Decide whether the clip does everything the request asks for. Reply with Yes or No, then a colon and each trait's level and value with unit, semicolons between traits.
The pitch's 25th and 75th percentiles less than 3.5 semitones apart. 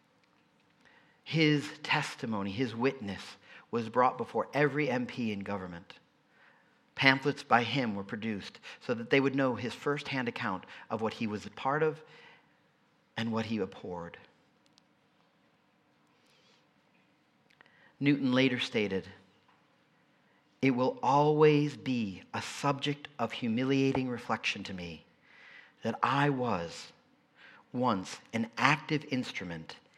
No: average, 4.3 semitones